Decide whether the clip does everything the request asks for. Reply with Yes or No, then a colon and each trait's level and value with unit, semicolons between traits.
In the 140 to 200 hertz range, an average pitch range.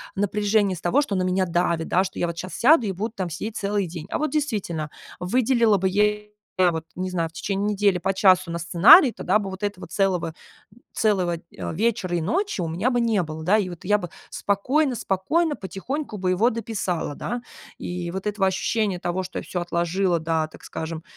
Yes: high, 190 Hz; average, 3.4 semitones